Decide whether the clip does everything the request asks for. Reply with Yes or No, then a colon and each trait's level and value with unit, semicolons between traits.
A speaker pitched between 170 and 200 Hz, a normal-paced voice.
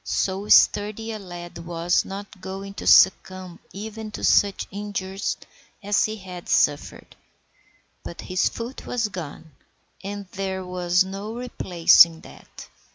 No: high, 190 Hz; slow, 130 wpm